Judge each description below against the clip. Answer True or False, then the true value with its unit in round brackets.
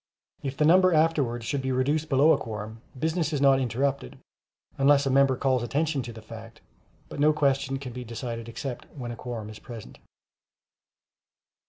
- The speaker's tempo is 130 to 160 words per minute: False (175 wpm)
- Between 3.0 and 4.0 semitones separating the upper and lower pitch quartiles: True (3.6 semitones)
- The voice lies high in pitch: False (135 Hz)